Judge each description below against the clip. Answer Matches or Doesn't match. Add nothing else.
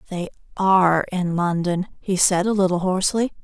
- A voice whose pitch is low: Doesn't match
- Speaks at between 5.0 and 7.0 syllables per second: Matches